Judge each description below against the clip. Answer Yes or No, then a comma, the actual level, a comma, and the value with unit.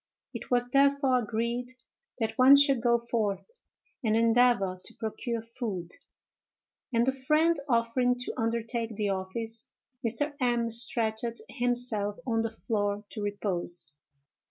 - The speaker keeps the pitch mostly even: Yes, narrow, 2.2 semitones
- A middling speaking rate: No, slow, 130 wpm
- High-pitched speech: Yes, high, 230 Hz